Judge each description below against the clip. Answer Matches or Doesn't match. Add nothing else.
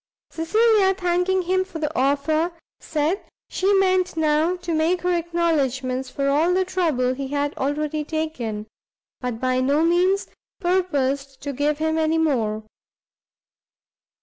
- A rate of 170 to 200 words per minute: Doesn't match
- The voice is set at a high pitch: Matches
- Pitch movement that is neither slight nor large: Matches